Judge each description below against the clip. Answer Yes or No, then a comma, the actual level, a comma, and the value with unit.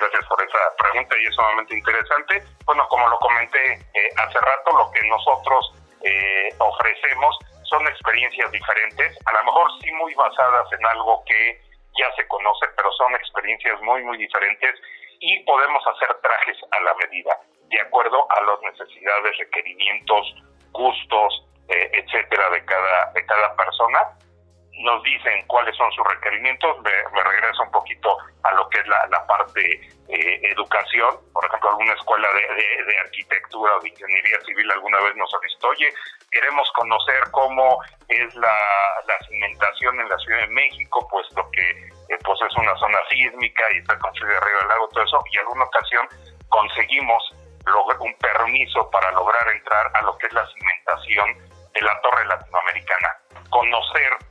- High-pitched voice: No, low, 100 Hz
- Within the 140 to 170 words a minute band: Yes, average, 165 wpm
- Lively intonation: Yes, wide, 7.3 semitones